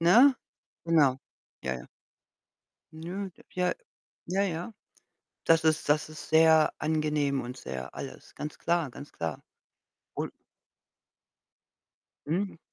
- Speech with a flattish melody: No, average, 3.1 semitones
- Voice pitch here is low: No, medium, 160 Hz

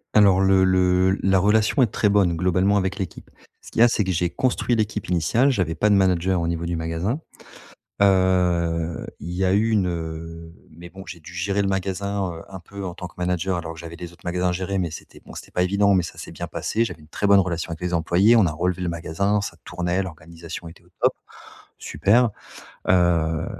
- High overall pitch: No, very low, 90 Hz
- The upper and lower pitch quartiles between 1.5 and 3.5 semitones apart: Yes, average, 2.7 semitones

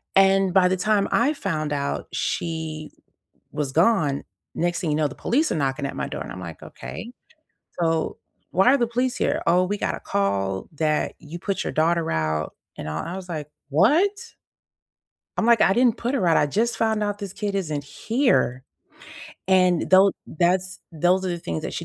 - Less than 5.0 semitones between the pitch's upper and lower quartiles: No, average, 5.3 semitones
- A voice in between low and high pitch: Yes, medium, 180 Hz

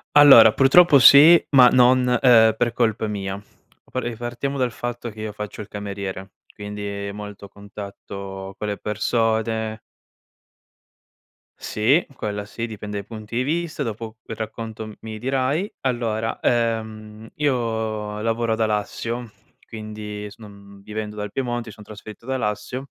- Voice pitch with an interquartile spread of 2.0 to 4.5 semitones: Yes, narrow, 2.5 semitones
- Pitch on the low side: Yes, low, 110 Hz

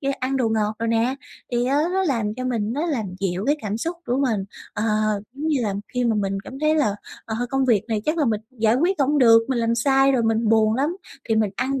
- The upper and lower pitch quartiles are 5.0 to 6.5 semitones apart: No, average, 3.8 semitones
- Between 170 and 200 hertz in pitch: No, high, 240 Hz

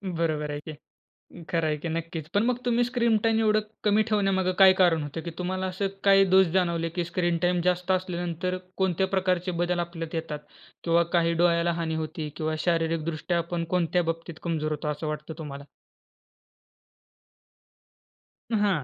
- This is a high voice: No, medium, 170 Hz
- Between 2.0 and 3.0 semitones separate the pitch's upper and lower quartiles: Yes, narrow, 2.5 semitones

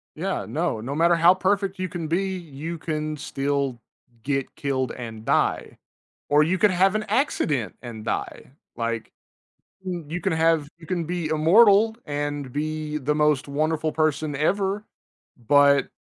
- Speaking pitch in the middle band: Yes, medium, 155 Hz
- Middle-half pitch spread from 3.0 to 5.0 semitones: Yes, average, 3.9 semitones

